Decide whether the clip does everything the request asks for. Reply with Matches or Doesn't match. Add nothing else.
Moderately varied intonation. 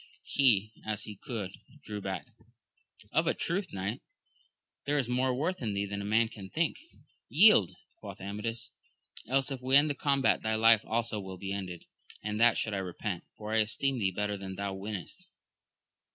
Matches